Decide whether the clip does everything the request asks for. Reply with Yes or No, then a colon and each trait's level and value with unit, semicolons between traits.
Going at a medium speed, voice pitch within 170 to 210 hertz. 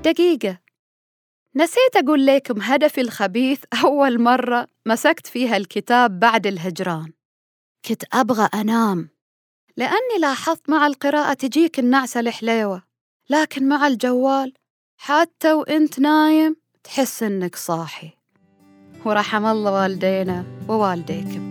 No: average, 100 wpm; high, 240 Hz